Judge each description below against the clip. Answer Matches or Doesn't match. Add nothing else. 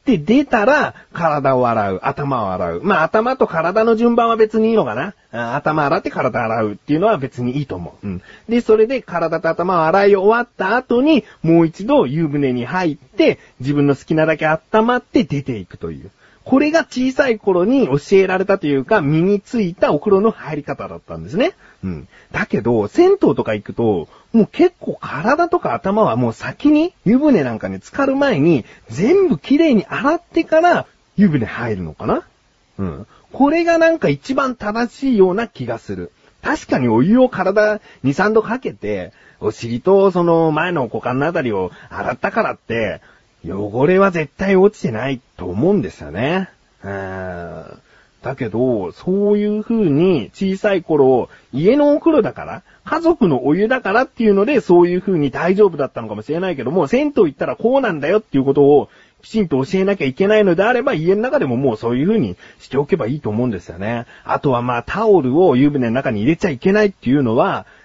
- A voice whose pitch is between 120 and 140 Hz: Doesn't match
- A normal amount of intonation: Doesn't match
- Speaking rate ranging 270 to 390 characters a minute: Matches